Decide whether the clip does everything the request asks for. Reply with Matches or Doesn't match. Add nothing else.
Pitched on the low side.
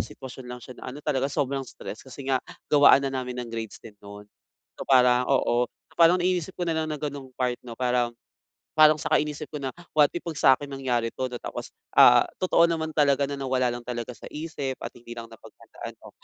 Matches